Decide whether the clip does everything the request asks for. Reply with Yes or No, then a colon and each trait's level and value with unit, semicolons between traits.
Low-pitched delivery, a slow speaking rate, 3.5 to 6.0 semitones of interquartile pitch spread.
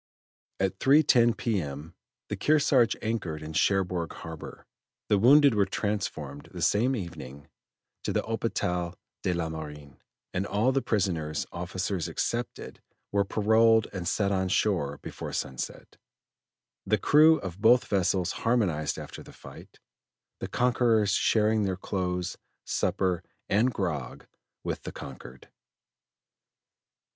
Yes: very low, 95 Hz; slow, 125 wpm; average, 5.2 semitones